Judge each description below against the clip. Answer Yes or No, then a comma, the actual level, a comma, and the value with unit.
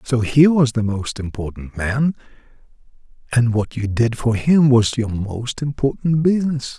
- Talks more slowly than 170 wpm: Yes, average, 160 wpm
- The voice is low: Yes, low, 125 Hz